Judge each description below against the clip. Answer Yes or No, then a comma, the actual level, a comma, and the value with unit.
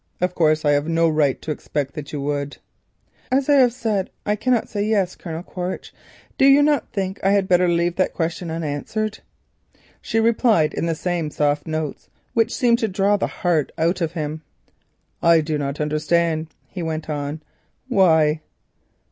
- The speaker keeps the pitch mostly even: No, average, 4.6 semitones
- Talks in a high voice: No, medium, 170 Hz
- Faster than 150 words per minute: Yes, average, 180 wpm